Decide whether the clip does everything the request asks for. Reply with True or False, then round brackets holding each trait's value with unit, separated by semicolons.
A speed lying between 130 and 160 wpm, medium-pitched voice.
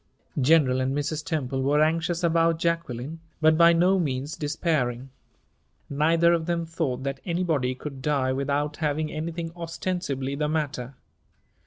True (140 wpm; 155 Hz)